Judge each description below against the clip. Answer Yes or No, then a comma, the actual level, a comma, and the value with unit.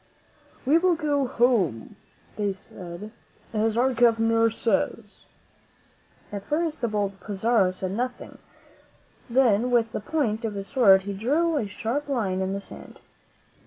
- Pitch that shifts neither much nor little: Yes, average, 4.3 semitones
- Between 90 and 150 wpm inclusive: Yes, average, 140 wpm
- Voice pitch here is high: Yes, high, 225 Hz